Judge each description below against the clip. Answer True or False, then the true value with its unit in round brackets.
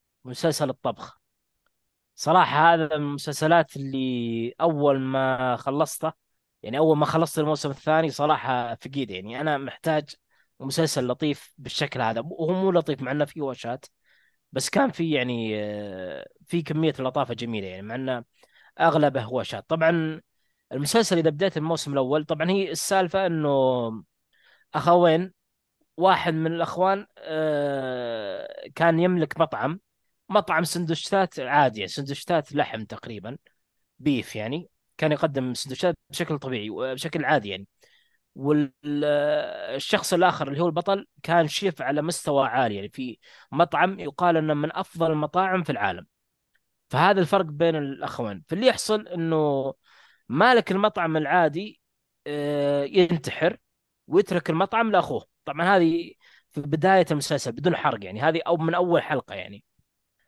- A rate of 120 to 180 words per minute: True (125 wpm)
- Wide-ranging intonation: False (4.3 semitones)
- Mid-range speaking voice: True (155 Hz)